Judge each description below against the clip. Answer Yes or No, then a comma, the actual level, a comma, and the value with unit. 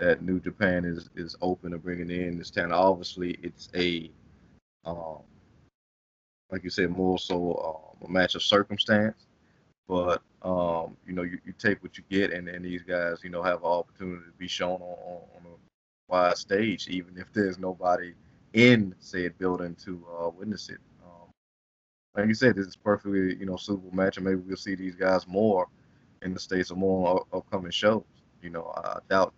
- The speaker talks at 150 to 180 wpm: No, average, 190 wpm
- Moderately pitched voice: No, very low, 90 Hz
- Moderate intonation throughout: No, narrow, 1.4 semitones